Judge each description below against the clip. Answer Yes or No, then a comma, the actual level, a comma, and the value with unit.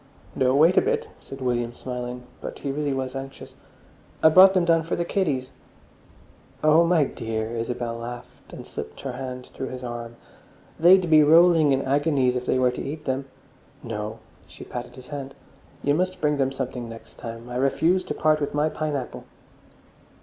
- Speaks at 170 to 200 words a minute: Yes, average, 175 wpm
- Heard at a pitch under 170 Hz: Yes, low, 135 Hz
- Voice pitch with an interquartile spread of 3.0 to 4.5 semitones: Yes, average, 4.0 semitones